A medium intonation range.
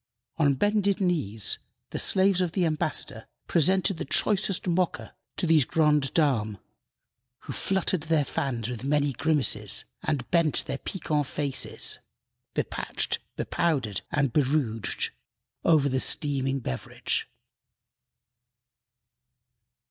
Yes: average, 4.4 semitones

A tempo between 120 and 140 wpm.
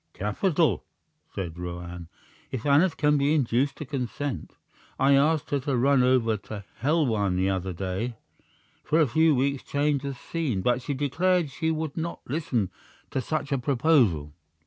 No: average, 160 wpm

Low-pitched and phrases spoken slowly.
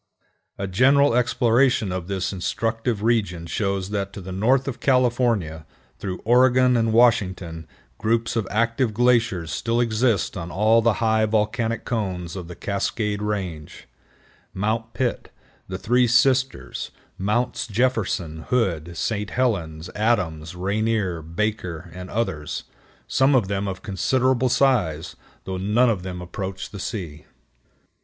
Yes: low, 105 Hz; slow, 130 wpm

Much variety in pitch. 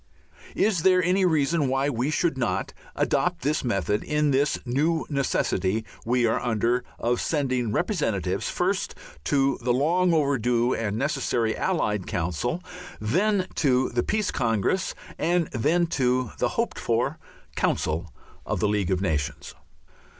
Yes: wide, 5.7 semitones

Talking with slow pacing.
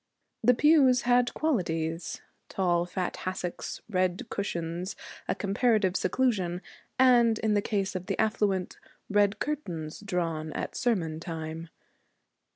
Yes: slow, 120 wpm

